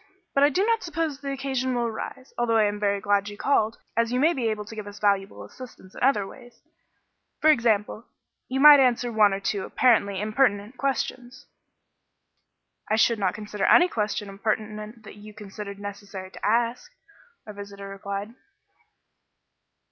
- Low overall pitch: No, high, 215 Hz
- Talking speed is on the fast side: No, average, 170 wpm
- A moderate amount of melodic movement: Yes, average, 3.9 semitones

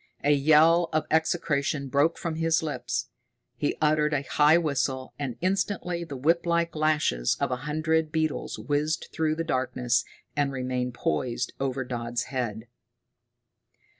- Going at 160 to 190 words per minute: No, slow, 135 wpm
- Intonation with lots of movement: No, average, 3.7 semitones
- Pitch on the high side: No, medium, 150 Hz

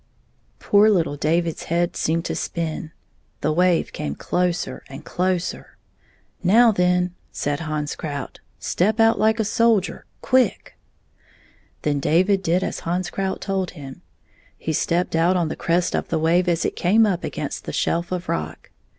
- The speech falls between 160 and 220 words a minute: Yes, average, 165 wpm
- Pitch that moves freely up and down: No, average, 2.8 semitones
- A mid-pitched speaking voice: Yes, medium, 175 Hz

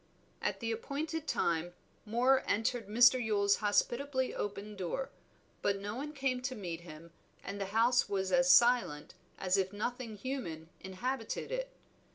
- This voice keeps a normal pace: Yes, average, 150 wpm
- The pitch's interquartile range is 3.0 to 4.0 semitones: No, average, 4.7 semitones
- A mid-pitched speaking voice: No, high, 225 Hz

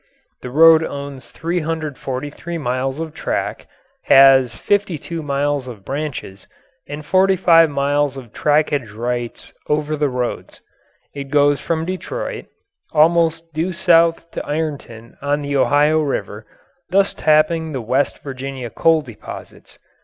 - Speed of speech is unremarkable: No, slow, 125 wpm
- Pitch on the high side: No, medium, 145 Hz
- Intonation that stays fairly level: No, average, 3.3 semitones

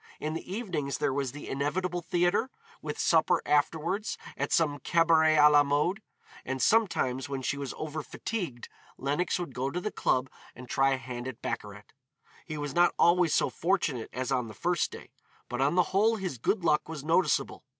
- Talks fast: No, average, 190 wpm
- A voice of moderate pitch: Yes, medium, 150 Hz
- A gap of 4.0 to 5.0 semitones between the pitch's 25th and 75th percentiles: Yes, average, 4.7 semitones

